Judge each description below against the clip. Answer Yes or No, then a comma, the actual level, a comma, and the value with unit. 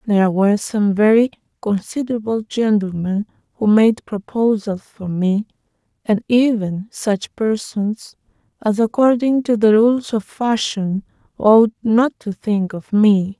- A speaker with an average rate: No, slow, 125 wpm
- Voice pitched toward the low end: No, high, 215 Hz